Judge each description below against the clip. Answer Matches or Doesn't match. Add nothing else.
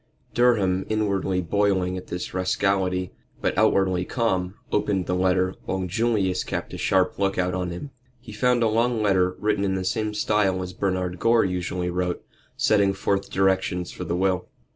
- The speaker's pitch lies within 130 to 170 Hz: Doesn't match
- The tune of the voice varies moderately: Doesn't match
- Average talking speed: Matches